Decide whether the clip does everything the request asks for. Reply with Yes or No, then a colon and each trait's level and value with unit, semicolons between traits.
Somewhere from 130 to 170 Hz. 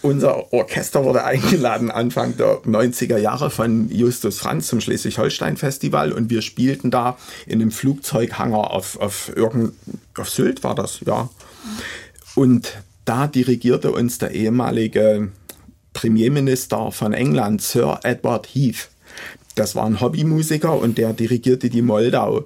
No: low, 120 Hz